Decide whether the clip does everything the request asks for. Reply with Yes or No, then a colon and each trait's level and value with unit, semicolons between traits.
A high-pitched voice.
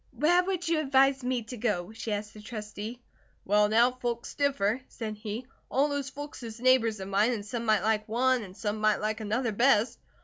Yes: high, 230 Hz